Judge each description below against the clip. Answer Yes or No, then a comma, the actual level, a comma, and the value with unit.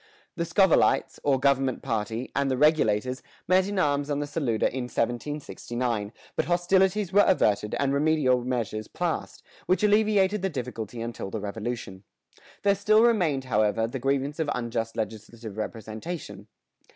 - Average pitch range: No, wide, 7.0 semitones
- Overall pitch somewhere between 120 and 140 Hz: Yes, low, 135 Hz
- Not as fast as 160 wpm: Yes, average, 145 wpm